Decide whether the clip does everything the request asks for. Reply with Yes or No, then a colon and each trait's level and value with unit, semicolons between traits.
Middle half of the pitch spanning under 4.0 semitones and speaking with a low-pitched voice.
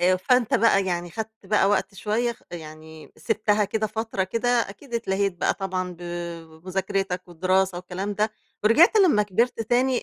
No: average, 3.5 semitones; high, 200 Hz